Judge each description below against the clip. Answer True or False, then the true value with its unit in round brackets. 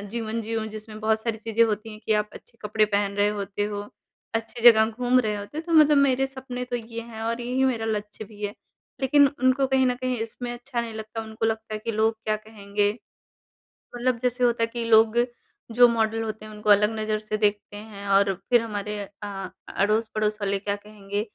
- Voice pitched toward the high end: True (220 Hz)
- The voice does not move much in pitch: True (2.2 semitones)